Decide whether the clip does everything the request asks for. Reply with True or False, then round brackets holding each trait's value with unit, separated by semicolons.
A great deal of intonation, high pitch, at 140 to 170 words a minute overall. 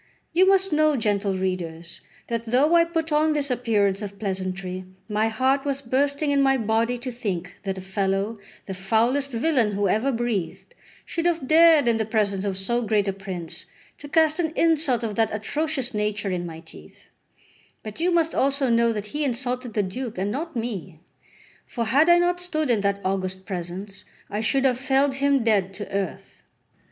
False (6.1 semitones; 230 Hz; 185 wpm)